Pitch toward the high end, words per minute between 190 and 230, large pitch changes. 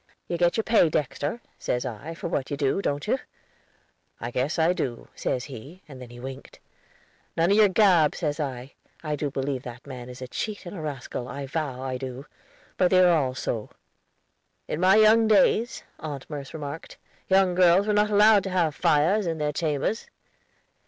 No: medium, 150 Hz; average, 195 wpm; wide, 5.7 semitones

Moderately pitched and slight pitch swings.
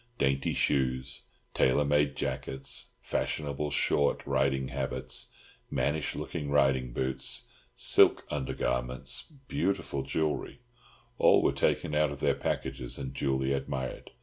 No: very low, 70 Hz; narrow, 1.7 semitones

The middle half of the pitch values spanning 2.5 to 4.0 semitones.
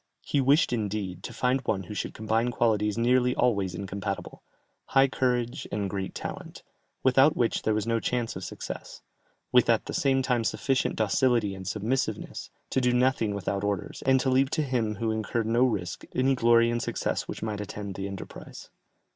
Yes: average, 3.7 semitones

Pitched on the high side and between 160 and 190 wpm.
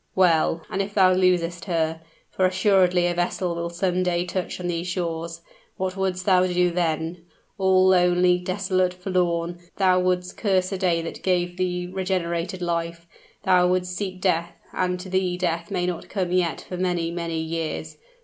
No: medium, 180 Hz; average, 170 wpm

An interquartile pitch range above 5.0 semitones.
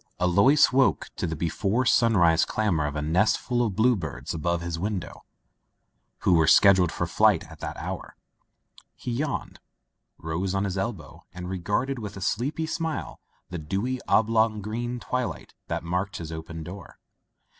Yes: wide, 5.5 semitones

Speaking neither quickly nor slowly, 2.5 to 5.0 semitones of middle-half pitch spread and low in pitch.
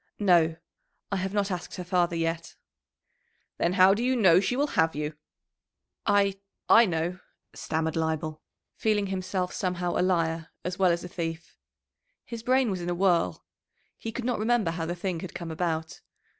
No: average, 175 wpm; average, 3.2 semitones; medium, 180 Hz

